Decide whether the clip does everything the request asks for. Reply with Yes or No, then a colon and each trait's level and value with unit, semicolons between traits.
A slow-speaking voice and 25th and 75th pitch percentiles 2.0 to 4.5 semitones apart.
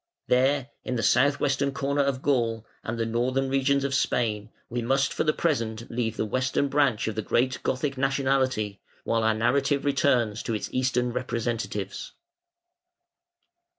No: average, 155 wpm; average, 3.2 semitones